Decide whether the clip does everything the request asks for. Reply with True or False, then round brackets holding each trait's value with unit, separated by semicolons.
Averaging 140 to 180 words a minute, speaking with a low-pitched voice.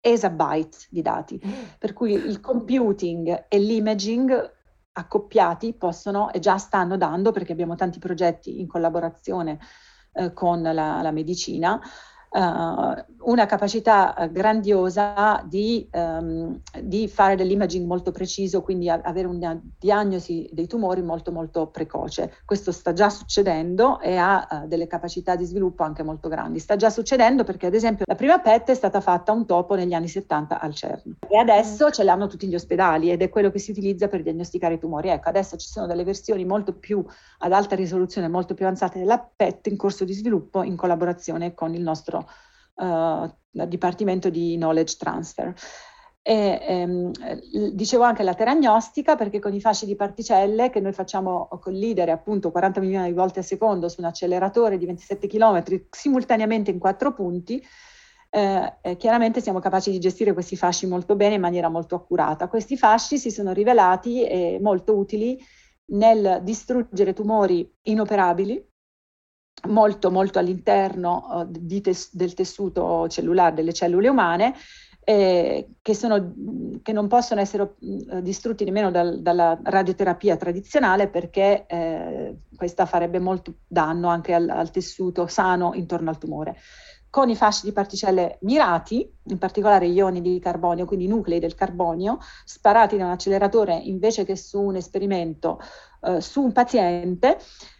False (155 wpm; 190 Hz)